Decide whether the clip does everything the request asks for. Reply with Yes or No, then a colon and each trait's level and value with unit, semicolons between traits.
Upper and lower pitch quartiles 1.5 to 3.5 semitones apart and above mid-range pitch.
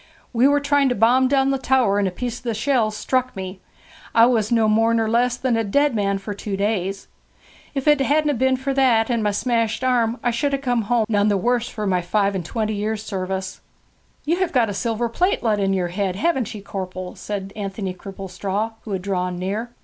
No: average, 4.1 semitones; high, 225 Hz